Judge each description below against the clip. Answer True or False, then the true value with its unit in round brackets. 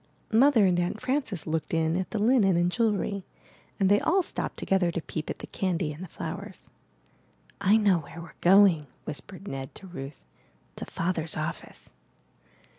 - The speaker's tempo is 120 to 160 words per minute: False (170 wpm)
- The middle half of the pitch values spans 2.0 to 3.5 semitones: False (3.9 semitones)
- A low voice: False (185 Hz)